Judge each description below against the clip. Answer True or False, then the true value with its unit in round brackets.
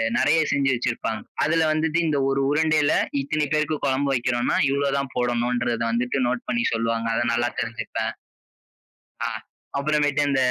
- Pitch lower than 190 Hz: True (135 Hz)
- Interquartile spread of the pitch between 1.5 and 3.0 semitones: False (3.8 semitones)